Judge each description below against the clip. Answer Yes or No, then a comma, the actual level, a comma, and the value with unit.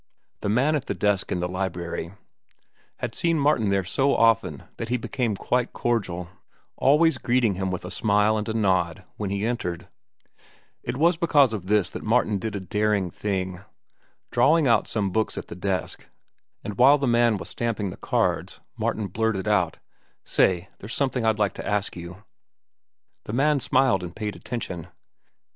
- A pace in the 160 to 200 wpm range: Yes, average, 175 wpm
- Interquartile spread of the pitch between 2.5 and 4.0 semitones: No, average, 4.4 semitones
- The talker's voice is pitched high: No, low, 105 Hz